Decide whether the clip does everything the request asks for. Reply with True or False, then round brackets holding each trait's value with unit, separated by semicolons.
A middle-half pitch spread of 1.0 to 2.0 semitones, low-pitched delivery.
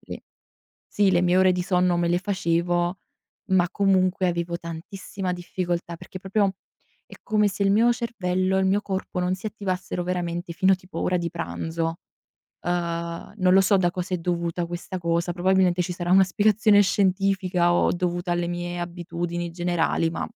False (1.7 semitones; 180 Hz)